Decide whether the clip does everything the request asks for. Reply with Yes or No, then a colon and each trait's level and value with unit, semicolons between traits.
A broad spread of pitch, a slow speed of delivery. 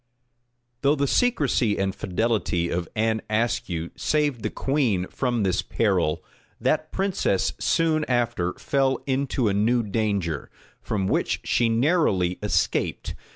Yes: wide, 6.0 semitones; slow, 125 wpm